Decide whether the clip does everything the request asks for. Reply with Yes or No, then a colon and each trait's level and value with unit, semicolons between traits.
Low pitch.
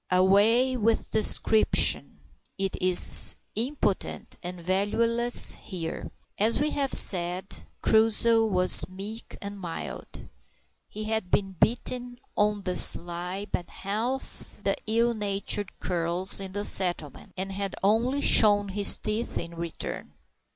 No: high, 200 Hz